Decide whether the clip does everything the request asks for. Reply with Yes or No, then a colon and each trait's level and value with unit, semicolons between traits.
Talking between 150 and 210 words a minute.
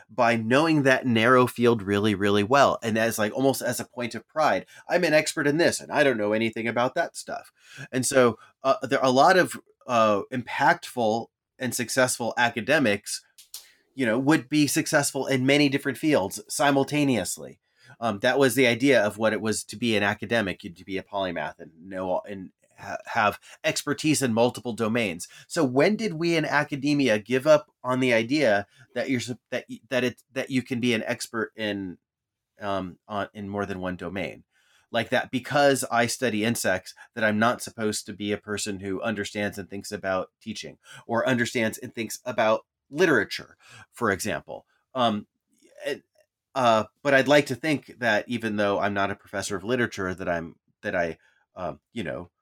Yes: average, 185 wpm